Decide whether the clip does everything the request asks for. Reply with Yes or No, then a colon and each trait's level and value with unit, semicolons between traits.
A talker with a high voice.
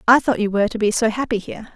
Yes: high, 220 Hz